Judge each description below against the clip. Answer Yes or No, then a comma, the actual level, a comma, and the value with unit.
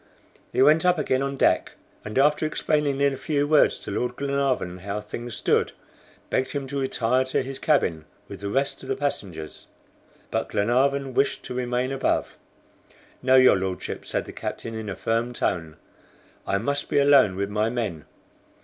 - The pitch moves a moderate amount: Yes, average, 4.8 semitones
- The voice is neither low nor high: No, low, 130 Hz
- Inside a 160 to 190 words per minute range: Yes, average, 175 wpm